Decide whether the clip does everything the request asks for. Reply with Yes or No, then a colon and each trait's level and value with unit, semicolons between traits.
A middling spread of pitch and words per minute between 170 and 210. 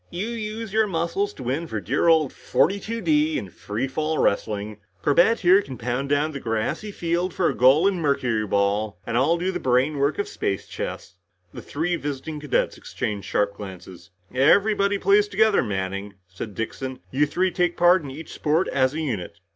No: wide, 7.9 semitones; average, 180 wpm